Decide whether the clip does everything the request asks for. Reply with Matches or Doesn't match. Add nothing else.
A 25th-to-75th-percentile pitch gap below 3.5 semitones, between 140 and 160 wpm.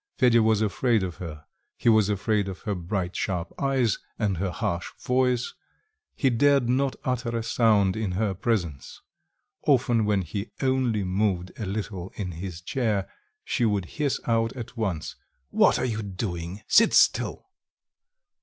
Doesn't match